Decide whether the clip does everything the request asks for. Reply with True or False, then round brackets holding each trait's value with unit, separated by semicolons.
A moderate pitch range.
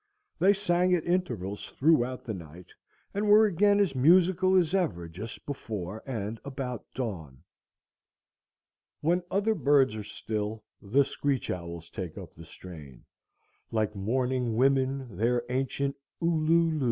False (8.3 semitones)